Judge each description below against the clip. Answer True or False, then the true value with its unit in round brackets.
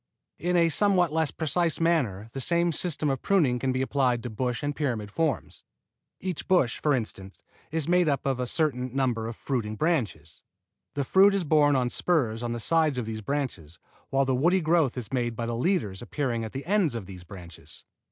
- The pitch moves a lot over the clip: True (5.7 semitones)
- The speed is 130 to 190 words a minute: False (200 wpm)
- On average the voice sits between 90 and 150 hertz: True (135 Hz)